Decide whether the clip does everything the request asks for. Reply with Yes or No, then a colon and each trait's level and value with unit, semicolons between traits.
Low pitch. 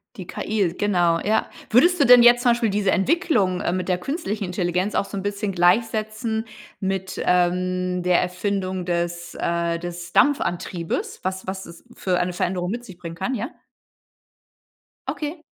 No: high, 190 Hz